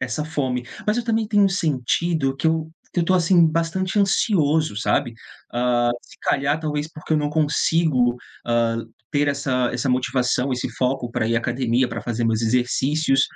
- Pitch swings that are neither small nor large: Yes, average, 4.8 semitones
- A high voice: No, medium, 140 Hz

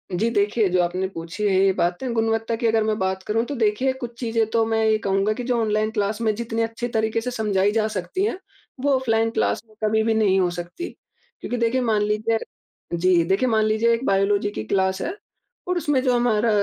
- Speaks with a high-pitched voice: Yes, high, 220 Hz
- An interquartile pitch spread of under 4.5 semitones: Yes, average, 2.8 semitones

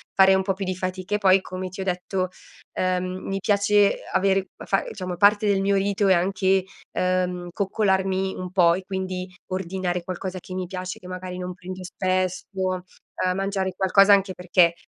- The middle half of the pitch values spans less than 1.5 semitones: Yes, narrow, 1.0 semitones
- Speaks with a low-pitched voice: No, medium, 185 Hz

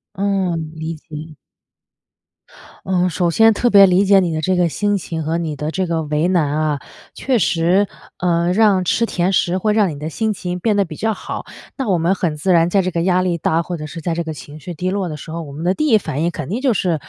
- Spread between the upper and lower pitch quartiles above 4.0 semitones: No, average, 3.4 semitones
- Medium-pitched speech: Yes, medium, 175 Hz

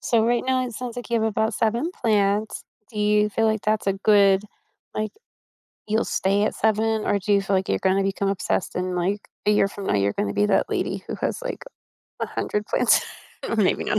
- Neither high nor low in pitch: No, high, 210 Hz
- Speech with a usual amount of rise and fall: No, narrow, 2.1 semitones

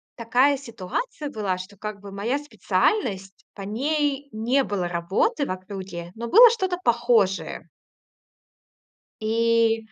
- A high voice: Yes, high, 225 Hz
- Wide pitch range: Yes, wide, 6.2 semitones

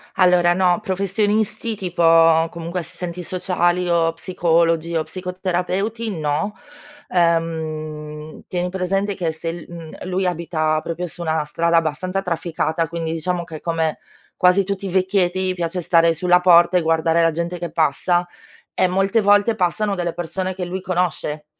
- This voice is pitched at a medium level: Yes, medium, 175 Hz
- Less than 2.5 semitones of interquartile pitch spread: Yes, narrow, 2.0 semitones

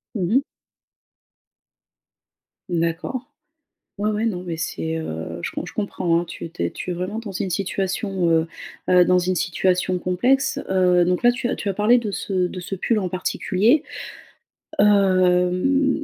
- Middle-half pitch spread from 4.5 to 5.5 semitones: No, average, 3.0 semitones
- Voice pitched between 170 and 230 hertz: Yes, medium, 185 Hz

